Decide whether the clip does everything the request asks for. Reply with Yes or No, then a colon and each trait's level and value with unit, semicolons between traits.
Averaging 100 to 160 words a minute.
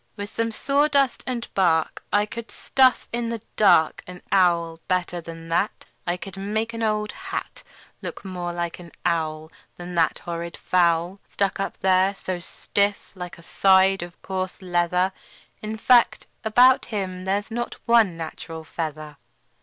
Yes: average, 155 wpm